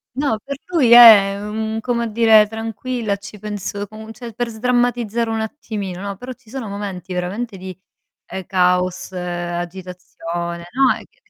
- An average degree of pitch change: Yes, average, 3.9 semitones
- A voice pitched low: No, high, 215 Hz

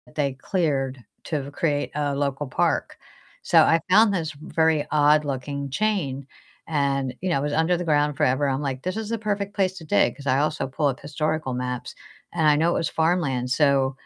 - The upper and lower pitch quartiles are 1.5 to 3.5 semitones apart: Yes, average, 3.1 semitones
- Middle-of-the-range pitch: Yes, medium, 150 Hz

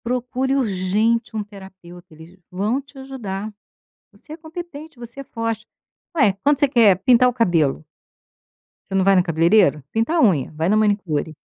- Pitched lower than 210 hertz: No, high, 215 Hz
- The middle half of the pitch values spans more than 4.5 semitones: Yes, wide, 5.6 semitones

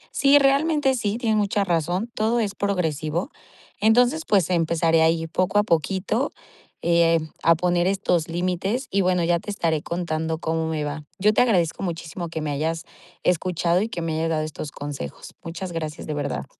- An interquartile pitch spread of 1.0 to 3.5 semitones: No, average, 4.0 semitones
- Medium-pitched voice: Yes, medium, 175 Hz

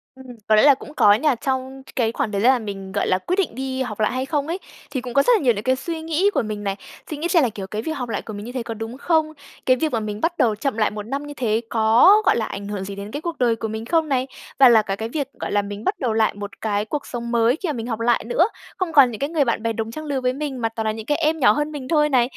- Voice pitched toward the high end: Yes, high, 245 Hz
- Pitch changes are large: No, average, 4.9 semitones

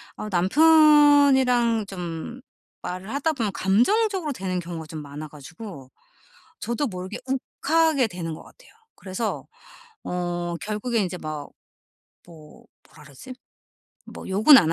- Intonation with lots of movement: Yes, wide, 7.5 semitones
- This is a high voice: Yes, high, 200 Hz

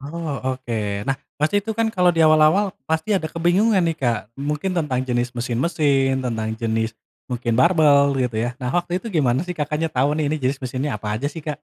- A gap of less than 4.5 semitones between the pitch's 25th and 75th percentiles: No, average, 5.0 semitones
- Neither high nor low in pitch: Yes, medium, 145 Hz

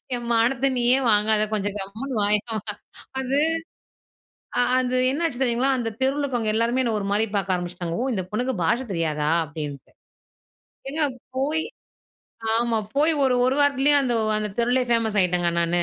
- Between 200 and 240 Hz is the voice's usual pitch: Yes, high, 235 Hz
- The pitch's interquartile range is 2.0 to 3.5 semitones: No, average, 4.7 semitones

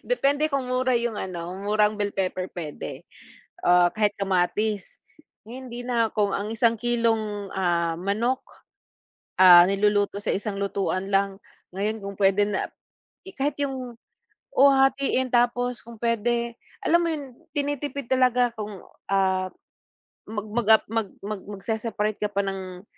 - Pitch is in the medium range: No, high, 215 Hz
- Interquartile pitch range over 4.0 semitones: No, average, 3.7 semitones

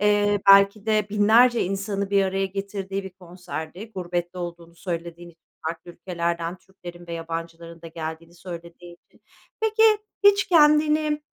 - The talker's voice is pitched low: No, medium, 185 Hz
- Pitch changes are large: No, average, 3.3 semitones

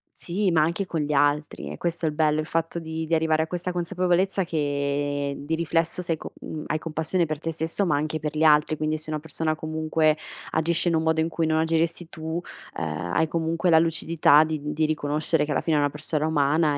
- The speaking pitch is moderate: Yes, medium, 160 Hz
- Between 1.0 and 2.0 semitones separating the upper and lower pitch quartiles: Yes, narrow, 1.4 semitones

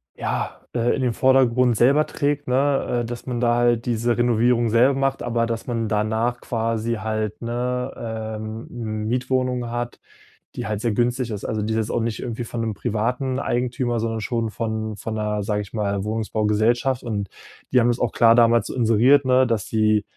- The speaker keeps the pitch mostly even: Yes, narrow, 2.0 semitones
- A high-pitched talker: No, low, 115 Hz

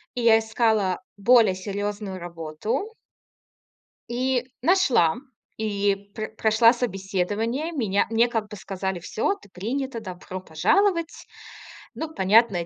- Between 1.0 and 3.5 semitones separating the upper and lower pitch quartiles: No, average, 4.2 semitones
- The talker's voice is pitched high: Yes, high, 215 Hz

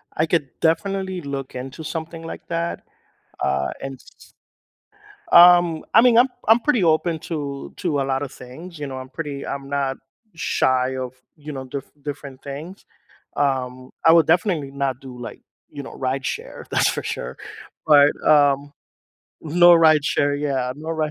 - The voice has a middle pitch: Yes, medium, 145 Hz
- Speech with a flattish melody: No, average, 3.6 semitones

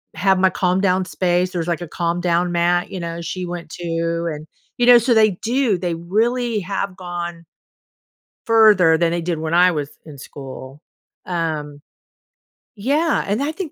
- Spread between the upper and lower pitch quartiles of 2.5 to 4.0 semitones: Yes, average, 3.2 semitones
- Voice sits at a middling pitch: Yes, medium, 175 Hz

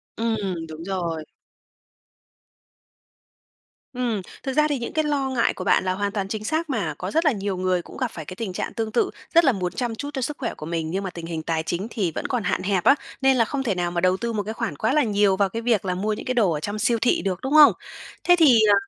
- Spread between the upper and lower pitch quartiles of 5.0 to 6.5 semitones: Yes, wide, 5.4 semitones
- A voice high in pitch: Yes, high, 210 Hz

